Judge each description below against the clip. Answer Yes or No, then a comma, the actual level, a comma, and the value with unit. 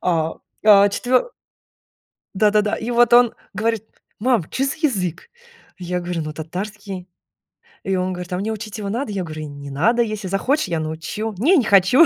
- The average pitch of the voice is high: Yes, high, 200 Hz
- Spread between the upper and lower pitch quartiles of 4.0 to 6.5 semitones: Yes, average, 4.3 semitones